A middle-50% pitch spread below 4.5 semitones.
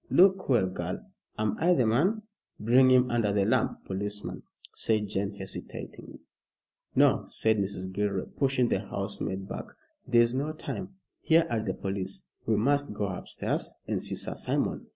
No: average, 5.0 semitones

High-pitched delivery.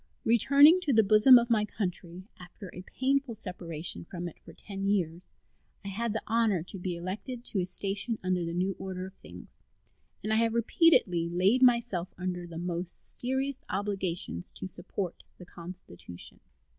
Yes: high, 195 Hz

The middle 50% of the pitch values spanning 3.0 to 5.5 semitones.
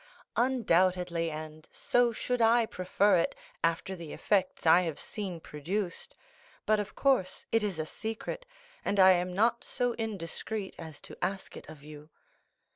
Yes: average, 4.8 semitones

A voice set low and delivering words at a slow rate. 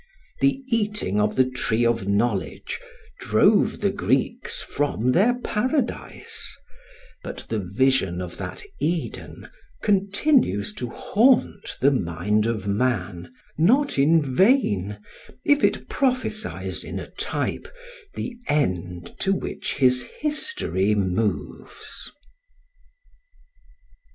Yes: low, 130 Hz; slow, 105 wpm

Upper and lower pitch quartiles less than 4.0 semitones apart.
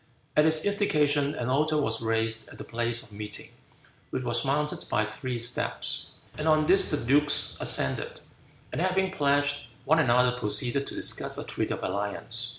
No: average, 4.5 semitones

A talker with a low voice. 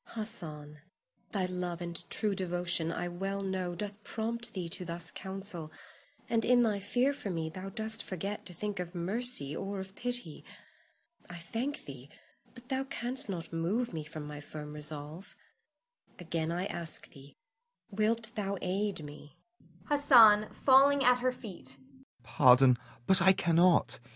No: high, 190 Hz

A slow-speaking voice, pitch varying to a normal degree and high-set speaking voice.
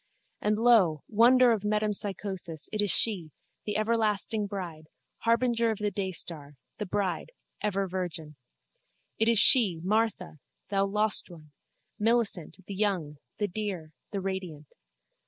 Yes: slow, 130 wpm; average, 3.5 semitones; high, 200 Hz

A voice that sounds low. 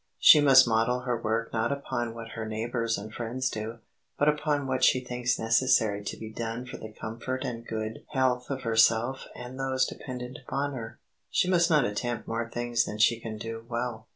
Yes: low, 120 Hz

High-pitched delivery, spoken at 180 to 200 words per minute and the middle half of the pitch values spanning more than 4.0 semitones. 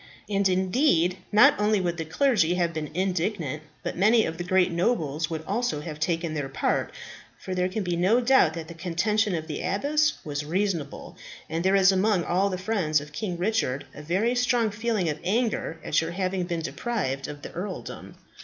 No: medium, 180 Hz; average, 195 wpm; average, 4.4 semitones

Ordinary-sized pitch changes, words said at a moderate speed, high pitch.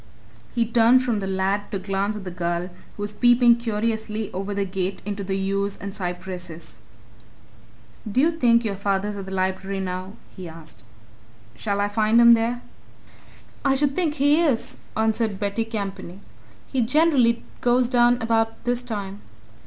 Yes: average, 3.6 semitones; average, 165 wpm; high, 210 Hz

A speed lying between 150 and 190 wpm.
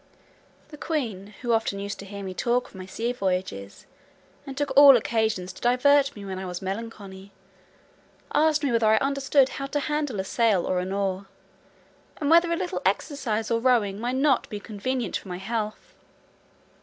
Yes: average, 180 wpm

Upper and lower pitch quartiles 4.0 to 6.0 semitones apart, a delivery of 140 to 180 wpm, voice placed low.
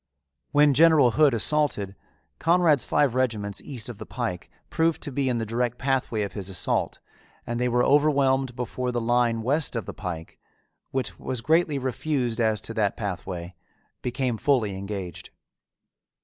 Yes: average, 4.3 semitones; average, 160 wpm; low, 125 Hz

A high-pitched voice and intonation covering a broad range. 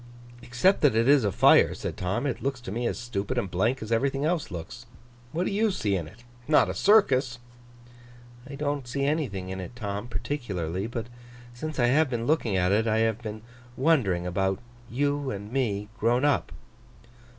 No: low, 120 Hz; wide, 5.7 semitones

